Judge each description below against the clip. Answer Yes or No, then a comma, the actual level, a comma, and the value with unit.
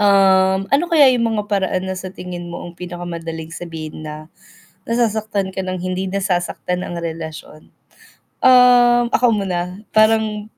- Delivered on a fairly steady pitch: No, average, 3.7 semitones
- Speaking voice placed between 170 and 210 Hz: Yes, high, 190 Hz